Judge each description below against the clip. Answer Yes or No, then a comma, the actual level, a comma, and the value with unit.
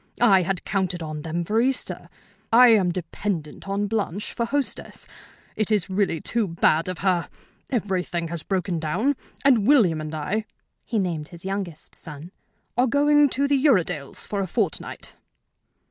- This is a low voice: No, high, 190 Hz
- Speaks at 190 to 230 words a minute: No, average, 160 wpm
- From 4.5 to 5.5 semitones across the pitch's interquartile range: Yes, average, 5.1 semitones